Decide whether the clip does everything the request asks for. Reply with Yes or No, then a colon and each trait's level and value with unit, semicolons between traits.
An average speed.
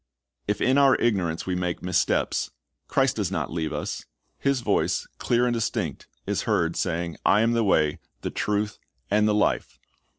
Yes: average, 170 wpm